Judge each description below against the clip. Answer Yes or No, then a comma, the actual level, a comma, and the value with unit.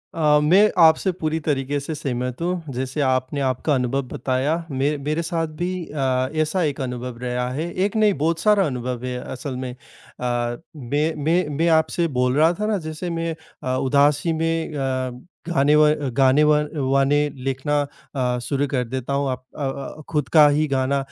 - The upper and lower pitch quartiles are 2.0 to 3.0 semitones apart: No, average, 3.4 semitones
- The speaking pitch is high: No, medium, 140 Hz